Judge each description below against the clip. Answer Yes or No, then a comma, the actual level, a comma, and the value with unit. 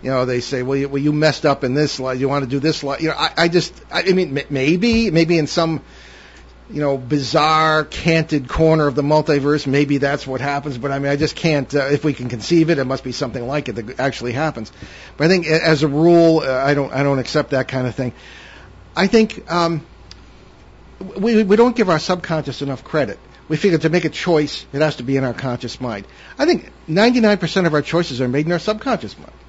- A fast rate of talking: Yes, fast, 240 wpm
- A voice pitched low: No, medium, 150 Hz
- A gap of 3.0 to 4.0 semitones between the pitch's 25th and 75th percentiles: Yes, average, 3.5 semitones